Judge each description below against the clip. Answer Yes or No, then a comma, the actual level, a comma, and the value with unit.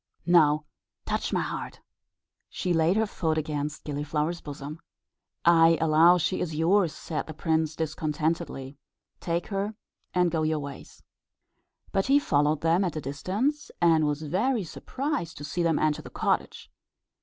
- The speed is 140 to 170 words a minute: Yes, average, 155 wpm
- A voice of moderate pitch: Yes, medium, 160 Hz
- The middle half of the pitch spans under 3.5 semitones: Yes, average, 2.8 semitones